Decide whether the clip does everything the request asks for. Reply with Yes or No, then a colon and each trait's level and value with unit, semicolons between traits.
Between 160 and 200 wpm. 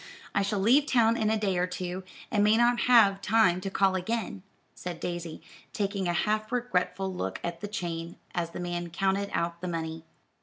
Yes: average, 195 wpm